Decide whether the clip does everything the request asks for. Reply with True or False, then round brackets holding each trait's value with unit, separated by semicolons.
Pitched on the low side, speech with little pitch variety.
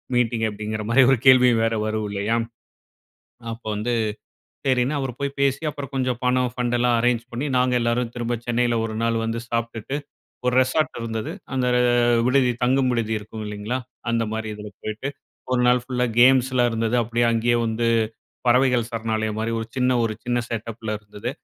True (120 Hz; 1.9 semitones)